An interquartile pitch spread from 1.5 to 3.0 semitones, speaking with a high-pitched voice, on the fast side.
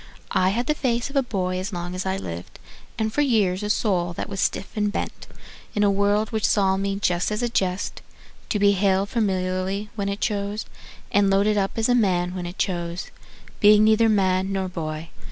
Yes: narrow, 2.4 semitones; high, 200 Hz; fast, 210 wpm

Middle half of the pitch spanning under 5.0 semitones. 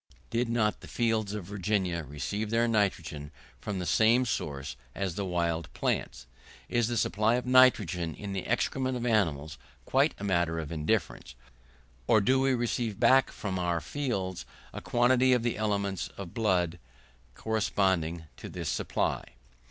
No: average, 5.3 semitones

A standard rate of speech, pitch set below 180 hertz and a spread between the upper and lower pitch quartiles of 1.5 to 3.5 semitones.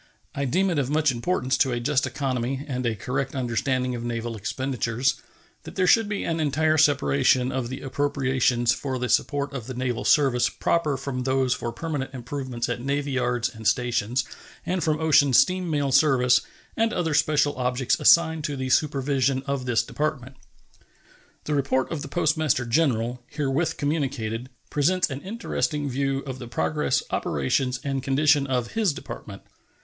Yes: average, 165 wpm; low, 135 Hz; average, 2.9 semitones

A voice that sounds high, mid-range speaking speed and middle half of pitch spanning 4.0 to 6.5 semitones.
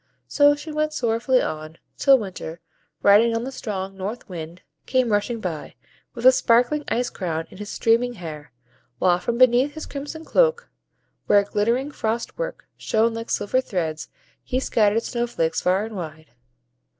Yes: high, 230 Hz; average, 160 wpm; wide, 5.6 semitones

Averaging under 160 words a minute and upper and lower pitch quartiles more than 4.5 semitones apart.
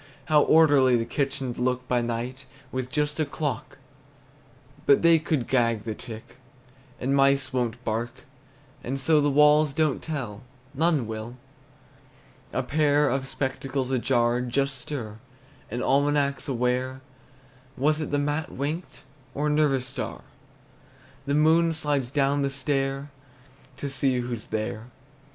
No: average, 140 wpm; average, 3.0 semitones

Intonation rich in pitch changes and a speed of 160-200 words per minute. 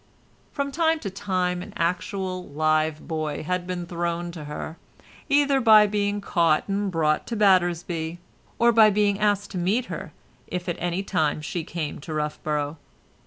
No: average, 4.2 semitones; average, 165 wpm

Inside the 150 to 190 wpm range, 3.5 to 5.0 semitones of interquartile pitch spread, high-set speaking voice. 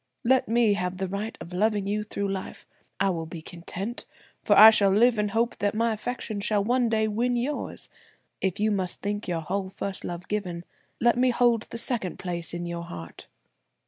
No: average, 200 wpm; average, 4.0 semitones; high, 205 Hz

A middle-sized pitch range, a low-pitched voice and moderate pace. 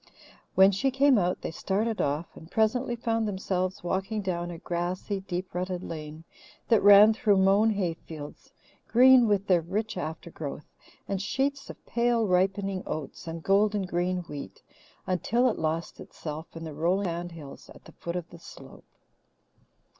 No: average, 3.9 semitones; medium, 185 Hz; average, 160 wpm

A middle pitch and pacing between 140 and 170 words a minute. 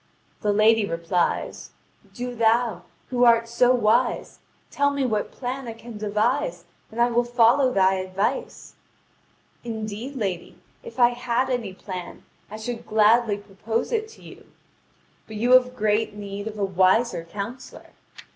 No: high, 225 Hz; average, 145 wpm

